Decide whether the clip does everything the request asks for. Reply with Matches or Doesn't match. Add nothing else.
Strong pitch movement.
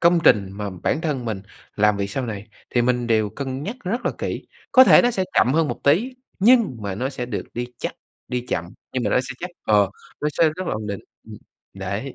Matches